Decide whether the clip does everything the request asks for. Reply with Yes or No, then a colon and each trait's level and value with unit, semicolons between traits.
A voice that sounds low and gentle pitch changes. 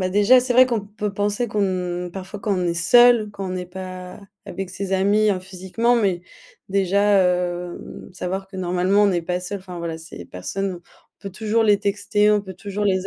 No: high, 195 Hz; narrow, 2.3 semitones